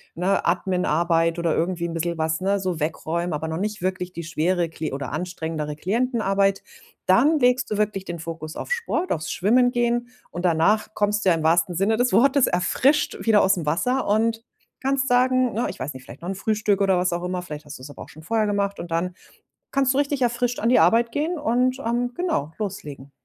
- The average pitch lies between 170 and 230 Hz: Yes, high, 190 Hz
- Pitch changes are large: Yes, wide, 6.2 semitones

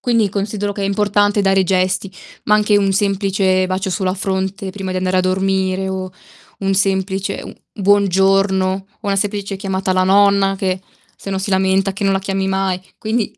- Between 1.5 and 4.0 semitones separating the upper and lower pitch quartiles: No, narrow, 0.9 semitones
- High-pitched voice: Yes, high, 195 Hz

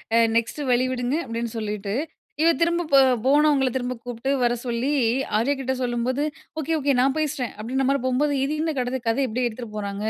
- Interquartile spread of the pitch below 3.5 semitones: Yes, average, 3.0 semitones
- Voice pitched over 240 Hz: Yes, very high, 255 Hz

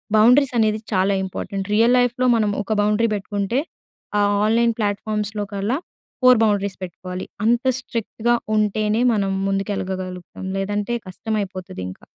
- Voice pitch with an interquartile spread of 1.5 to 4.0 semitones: Yes, average, 2.7 semitones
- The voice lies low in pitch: No, high, 210 Hz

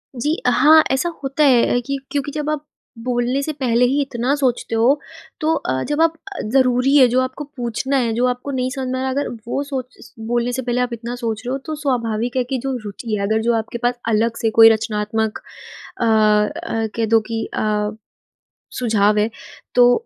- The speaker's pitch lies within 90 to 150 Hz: No, high, 245 Hz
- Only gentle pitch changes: No, average, 3.0 semitones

